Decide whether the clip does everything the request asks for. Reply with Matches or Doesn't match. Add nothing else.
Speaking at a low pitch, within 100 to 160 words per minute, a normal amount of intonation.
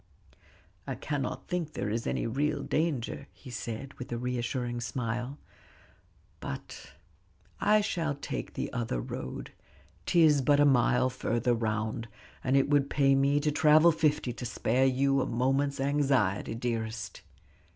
Matches